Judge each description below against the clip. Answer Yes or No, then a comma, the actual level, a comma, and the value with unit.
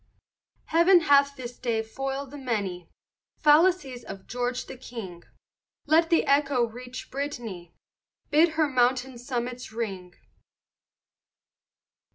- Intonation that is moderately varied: Yes, average, 3.6 semitones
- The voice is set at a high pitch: Yes, very high, 255 Hz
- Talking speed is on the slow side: Yes, slow, 110 wpm